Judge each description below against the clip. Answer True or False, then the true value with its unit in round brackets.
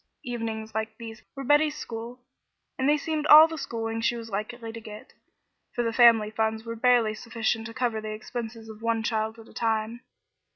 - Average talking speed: True (195 wpm)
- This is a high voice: True (230 Hz)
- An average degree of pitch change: False (1.6 semitones)